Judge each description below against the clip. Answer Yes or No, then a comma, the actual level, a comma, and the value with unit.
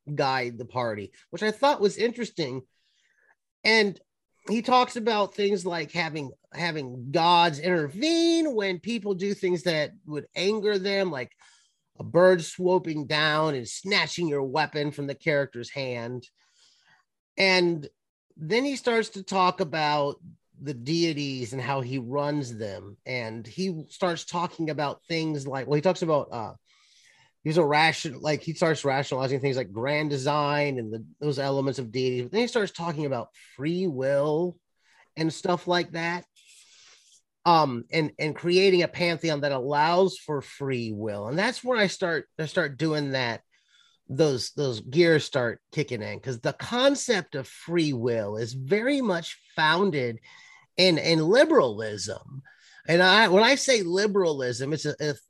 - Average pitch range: Yes, average, 5.0 semitones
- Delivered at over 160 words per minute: No, average, 155 wpm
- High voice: No, medium, 155 Hz